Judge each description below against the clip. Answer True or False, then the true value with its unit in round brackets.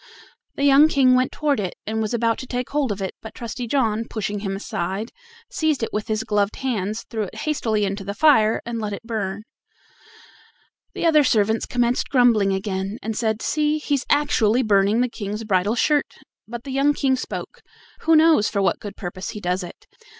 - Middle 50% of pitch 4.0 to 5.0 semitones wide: True (4.3 semitones)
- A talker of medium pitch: False (225 Hz)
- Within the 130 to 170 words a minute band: False (195 wpm)